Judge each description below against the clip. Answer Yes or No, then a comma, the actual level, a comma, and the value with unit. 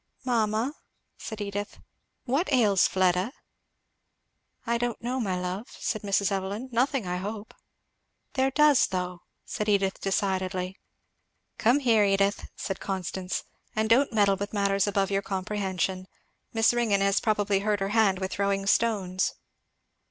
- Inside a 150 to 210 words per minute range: No, slow, 135 wpm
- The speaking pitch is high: Yes, high, 200 Hz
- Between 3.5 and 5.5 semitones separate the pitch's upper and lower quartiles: No, average, 2.7 semitones